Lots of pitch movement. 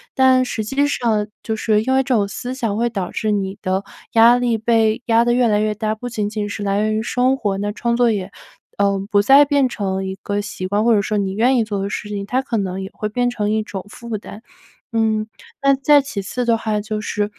No: average, 2.9 semitones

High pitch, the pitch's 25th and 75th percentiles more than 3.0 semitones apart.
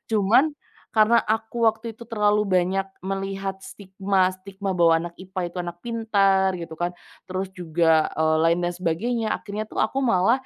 Yes: high, 195 Hz; average, 3.4 semitones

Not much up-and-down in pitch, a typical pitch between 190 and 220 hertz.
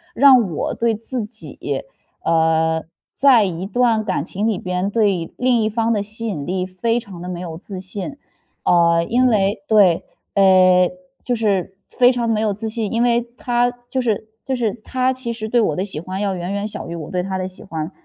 No: average, 4.2 semitones; high, 205 Hz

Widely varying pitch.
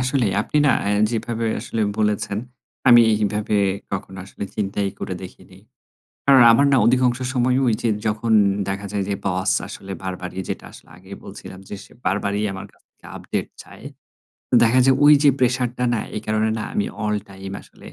No: average, 3.8 semitones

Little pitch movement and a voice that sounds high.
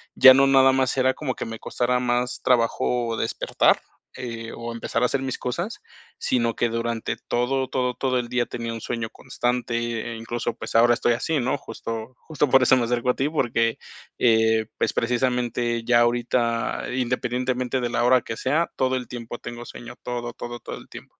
No: narrow, 1.5 semitones; low, 120 Hz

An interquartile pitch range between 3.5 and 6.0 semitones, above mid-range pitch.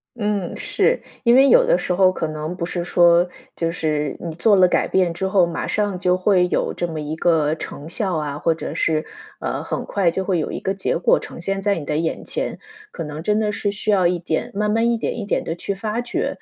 No: average, 3.8 semitones; medium, 180 Hz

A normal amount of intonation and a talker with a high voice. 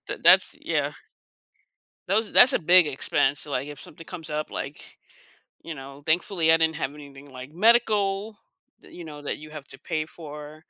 No: average, 3.4 semitones; medium, 155 Hz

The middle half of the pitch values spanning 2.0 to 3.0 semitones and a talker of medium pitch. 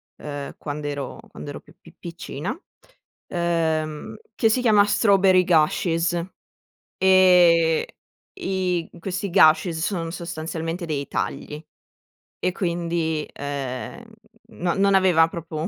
Yes: average, 2.7 semitones; medium, 170 Hz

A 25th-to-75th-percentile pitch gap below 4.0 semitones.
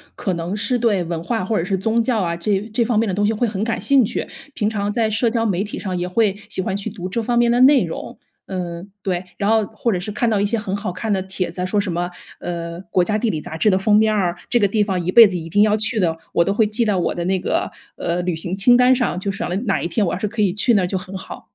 Yes: average, 3.4 semitones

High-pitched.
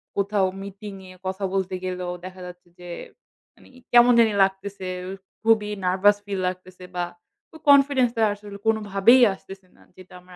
Yes: high, 195 Hz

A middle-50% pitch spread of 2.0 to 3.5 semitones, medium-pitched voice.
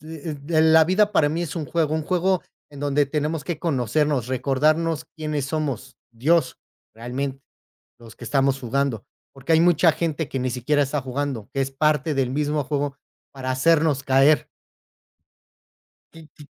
Yes: average, 2.8 semitones; medium, 145 Hz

